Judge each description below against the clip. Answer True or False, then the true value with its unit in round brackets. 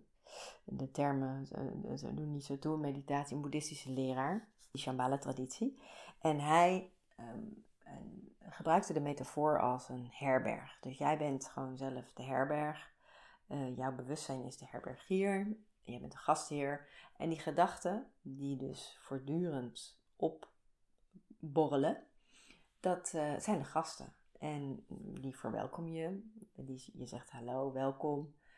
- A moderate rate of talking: False (130 wpm)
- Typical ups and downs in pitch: True (4.5 semitones)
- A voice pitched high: False (145 Hz)